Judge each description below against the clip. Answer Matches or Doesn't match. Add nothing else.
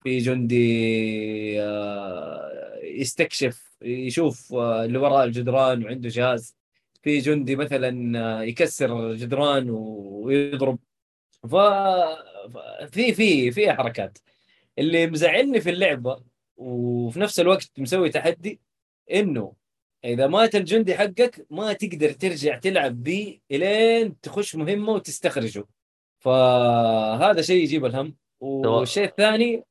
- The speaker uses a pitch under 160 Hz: Matches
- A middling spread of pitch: Doesn't match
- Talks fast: Doesn't match